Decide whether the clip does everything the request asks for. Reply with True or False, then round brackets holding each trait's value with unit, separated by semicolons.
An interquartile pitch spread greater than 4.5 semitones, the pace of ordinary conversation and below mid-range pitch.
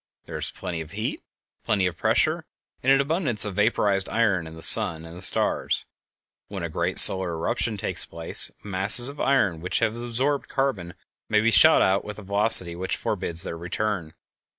True (5.1 semitones; 185 wpm; 100 Hz)